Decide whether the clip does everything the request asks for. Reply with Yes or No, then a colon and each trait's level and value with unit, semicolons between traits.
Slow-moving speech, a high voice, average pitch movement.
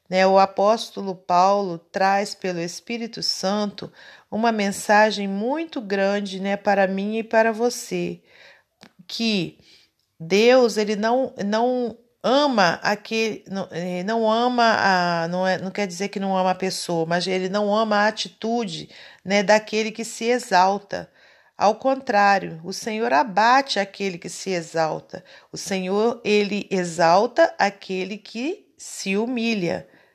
No: average, 130 wpm; high, 205 Hz; average, 3.2 semitones